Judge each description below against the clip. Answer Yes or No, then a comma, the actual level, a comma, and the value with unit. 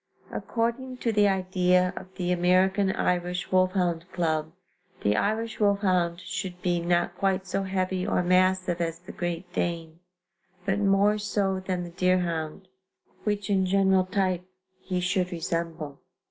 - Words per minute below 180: Yes, average, 140 wpm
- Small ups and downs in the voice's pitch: Yes, narrow, 1.8 semitones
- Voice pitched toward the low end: No, medium, 185 Hz